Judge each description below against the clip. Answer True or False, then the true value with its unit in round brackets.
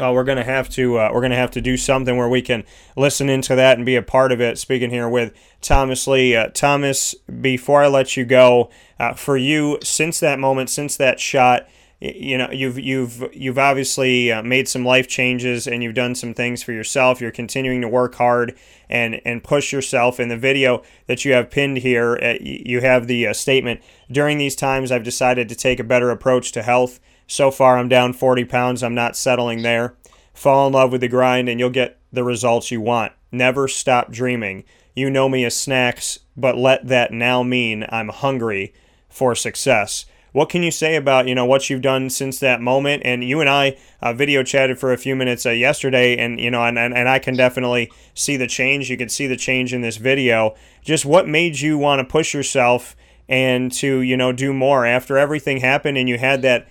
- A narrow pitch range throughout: True (1.6 semitones)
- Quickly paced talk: True (215 wpm)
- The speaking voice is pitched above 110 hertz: True (125 Hz)